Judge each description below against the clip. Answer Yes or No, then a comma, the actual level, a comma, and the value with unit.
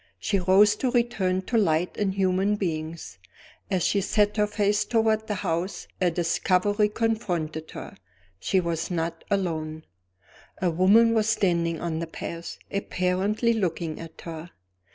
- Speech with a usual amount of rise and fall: Yes, average, 3.9 semitones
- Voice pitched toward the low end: No, medium, 185 Hz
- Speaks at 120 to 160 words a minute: Yes, average, 145 wpm